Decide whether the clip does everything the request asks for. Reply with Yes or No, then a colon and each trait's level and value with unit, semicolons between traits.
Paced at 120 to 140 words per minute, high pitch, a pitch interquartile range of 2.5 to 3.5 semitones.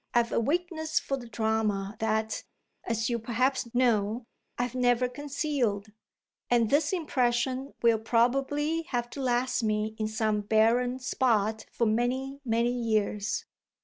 Yes: slow, 135 wpm; high, 240 Hz; average, 2.9 semitones